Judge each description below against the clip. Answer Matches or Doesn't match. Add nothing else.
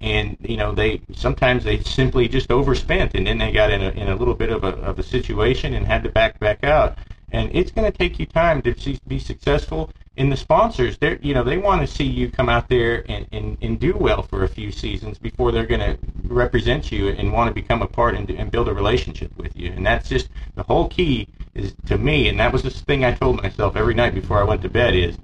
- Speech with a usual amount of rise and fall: Matches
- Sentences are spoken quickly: Matches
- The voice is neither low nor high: Doesn't match